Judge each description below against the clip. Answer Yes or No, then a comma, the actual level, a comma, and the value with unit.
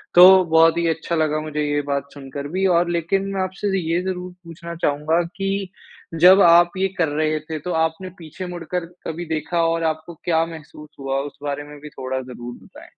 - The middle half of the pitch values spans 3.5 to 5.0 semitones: No, average, 2.9 semitones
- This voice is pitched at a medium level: Yes, medium, 165 Hz